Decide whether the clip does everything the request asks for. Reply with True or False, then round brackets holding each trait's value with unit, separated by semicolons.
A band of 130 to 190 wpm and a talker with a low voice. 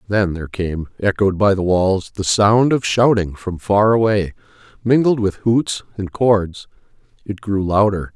True (160 wpm; 100 Hz)